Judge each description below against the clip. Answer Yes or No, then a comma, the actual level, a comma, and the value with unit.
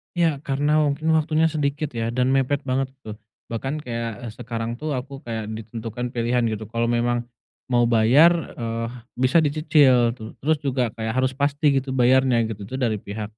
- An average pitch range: Yes, average, 3.6 semitones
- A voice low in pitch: Yes, low, 125 Hz